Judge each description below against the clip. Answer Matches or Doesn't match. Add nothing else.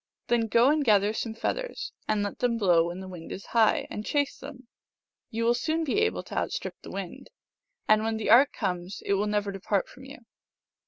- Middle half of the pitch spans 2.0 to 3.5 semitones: Doesn't match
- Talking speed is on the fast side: Matches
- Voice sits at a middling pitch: Doesn't match